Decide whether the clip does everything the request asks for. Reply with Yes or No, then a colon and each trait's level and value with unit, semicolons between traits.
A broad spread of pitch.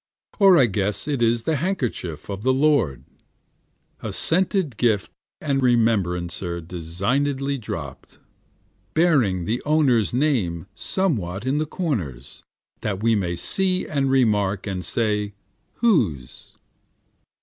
Yes: wide, 7.4 semitones